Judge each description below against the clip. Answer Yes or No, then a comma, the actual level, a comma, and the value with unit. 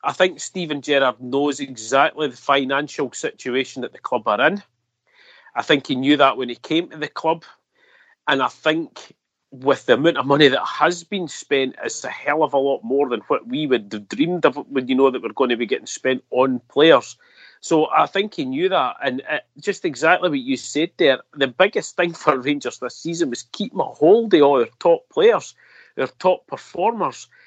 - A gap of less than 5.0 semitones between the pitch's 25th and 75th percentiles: No, average, 5.3 semitones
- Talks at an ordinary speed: No, fast, 210 wpm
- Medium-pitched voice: Yes, medium, 150 Hz